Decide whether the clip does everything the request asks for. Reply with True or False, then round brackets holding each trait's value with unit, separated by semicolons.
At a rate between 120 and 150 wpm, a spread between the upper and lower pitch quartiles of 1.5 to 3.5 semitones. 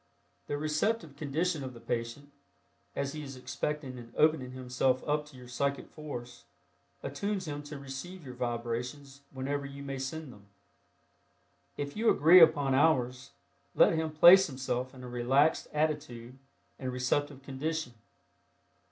True (145 wpm; 3.1 semitones)